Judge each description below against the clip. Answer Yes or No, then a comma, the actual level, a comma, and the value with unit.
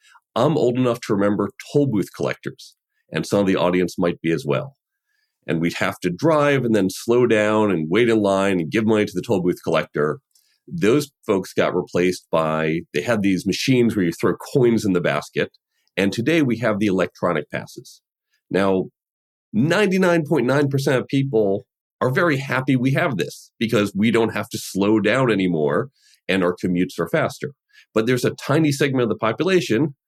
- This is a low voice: Yes, low, 110 Hz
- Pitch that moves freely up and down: Yes, wide, 6.5 semitones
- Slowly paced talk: No, average, 185 wpm